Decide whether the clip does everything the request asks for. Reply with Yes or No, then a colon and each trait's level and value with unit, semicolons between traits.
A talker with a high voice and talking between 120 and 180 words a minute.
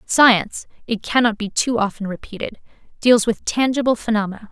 Yes: high, 225 Hz; average, 145 wpm